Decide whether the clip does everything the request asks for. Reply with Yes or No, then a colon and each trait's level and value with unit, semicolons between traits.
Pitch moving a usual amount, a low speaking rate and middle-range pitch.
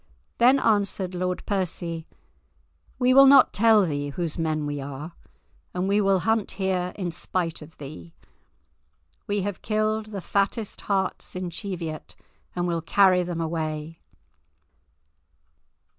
Yes: average, 3.8 semitones; slow, 130 wpm; medium, 180 Hz